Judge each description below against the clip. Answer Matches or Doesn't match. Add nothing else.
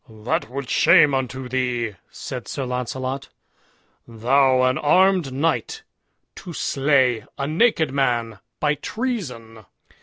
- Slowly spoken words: Matches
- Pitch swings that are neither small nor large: Matches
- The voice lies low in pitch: Matches